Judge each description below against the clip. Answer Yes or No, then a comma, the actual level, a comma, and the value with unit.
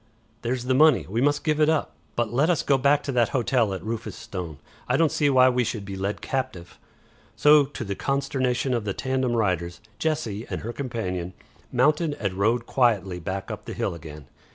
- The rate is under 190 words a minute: No, average, 200 wpm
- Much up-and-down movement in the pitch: Yes, wide, 5.7 semitones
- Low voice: Yes, low, 120 Hz